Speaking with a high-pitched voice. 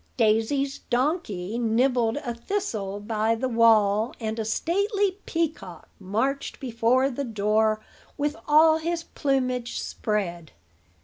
Yes: high, 235 Hz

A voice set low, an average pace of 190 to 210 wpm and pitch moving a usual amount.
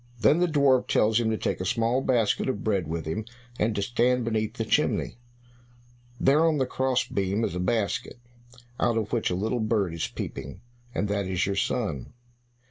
Yes: low, 110 Hz; average, 195 wpm; average, 3.9 semitones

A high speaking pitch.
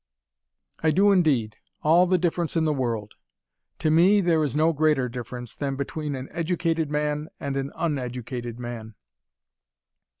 No: medium, 150 Hz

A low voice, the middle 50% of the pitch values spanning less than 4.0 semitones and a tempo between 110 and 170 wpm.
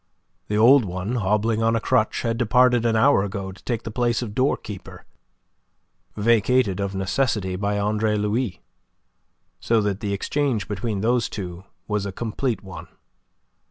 Yes: low, 110 Hz; average, 3.0 semitones; average, 155 wpm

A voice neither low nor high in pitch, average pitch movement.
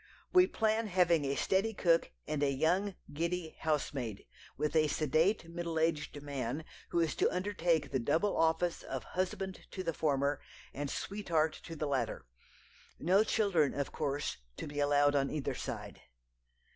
Yes: medium, 160 Hz; average, 3.9 semitones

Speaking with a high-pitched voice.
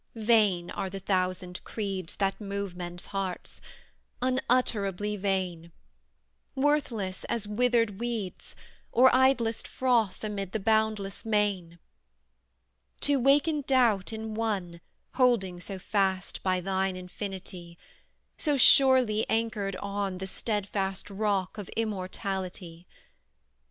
Yes: high, 200 Hz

